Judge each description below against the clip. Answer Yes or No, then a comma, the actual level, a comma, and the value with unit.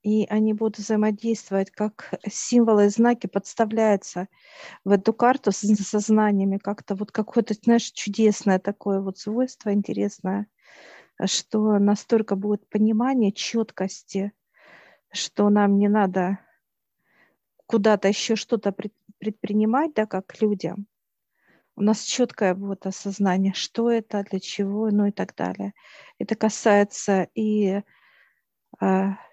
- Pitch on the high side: Yes, high, 210 Hz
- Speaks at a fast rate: No, average, 115 wpm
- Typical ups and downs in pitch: No, narrow, 1.8 semitones